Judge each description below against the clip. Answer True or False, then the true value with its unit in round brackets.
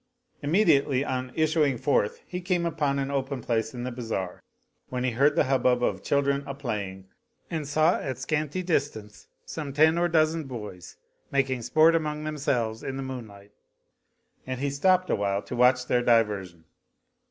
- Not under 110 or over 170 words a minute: True (165 wpm)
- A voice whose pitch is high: False (135 Hz)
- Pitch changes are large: False (4.3 semitones)